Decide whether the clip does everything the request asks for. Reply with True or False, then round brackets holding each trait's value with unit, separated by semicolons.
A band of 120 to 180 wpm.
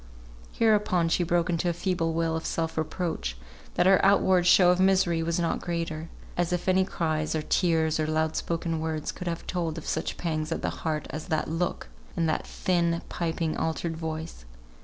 False (190 wpm)